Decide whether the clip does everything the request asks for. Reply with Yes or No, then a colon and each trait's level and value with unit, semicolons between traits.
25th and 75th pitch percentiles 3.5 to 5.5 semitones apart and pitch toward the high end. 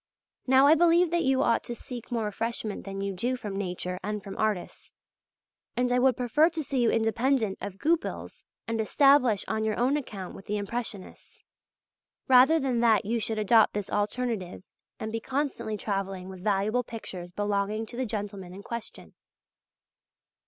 Yes: average, 3.8 semitones; high, 220 Hz